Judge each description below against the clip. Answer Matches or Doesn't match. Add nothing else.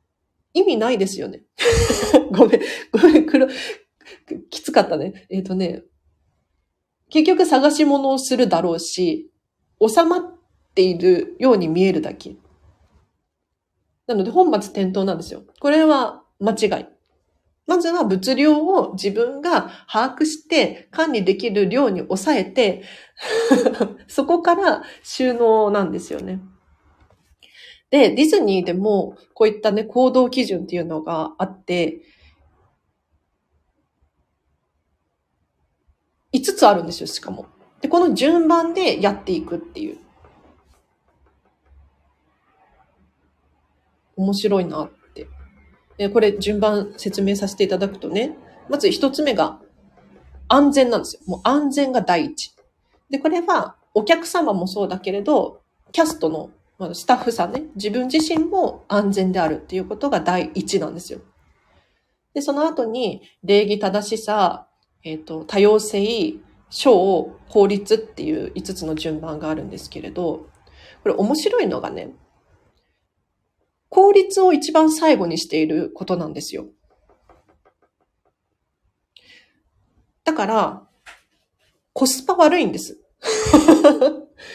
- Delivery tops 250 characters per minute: Doesn't match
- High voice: Matches